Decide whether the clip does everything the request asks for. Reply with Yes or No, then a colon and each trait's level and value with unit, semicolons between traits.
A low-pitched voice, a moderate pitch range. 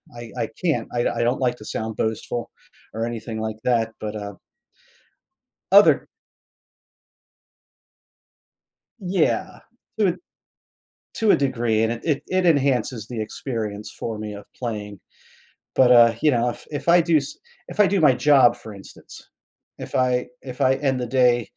Yes: low, 120 Hz; average, 3.6 semitones